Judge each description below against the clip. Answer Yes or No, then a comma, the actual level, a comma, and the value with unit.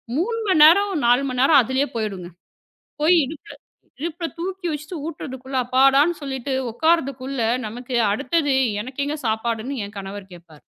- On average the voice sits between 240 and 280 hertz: Yes, very high, 270 Hz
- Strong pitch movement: No, average, 4.9 semitones